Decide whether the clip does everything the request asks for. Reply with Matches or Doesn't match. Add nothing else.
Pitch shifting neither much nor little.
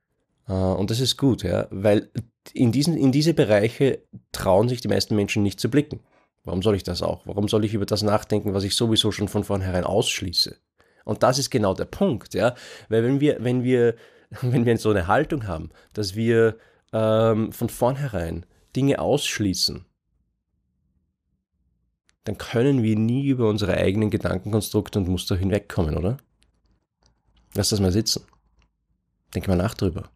Matches